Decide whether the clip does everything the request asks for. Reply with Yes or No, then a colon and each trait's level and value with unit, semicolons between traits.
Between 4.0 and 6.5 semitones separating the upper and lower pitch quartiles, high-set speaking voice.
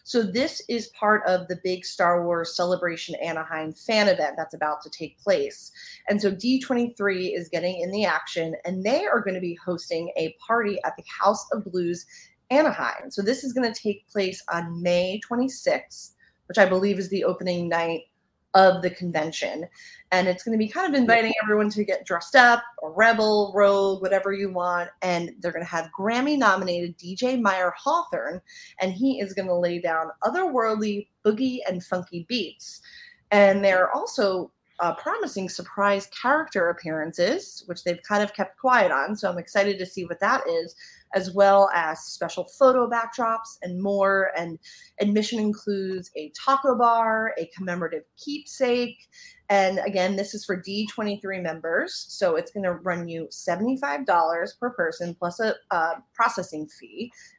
Yes: average, 4.8 semitones; high, 195 Hz